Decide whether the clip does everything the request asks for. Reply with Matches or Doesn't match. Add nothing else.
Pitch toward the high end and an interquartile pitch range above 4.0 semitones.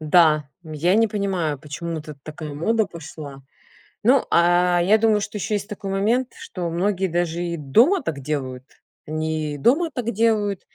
Doesn't match